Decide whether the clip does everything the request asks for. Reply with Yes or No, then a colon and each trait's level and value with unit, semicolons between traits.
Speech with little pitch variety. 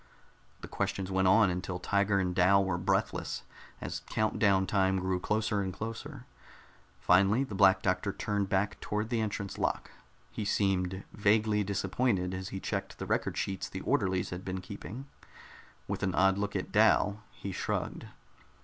Yes: narrow, 1.9 semitones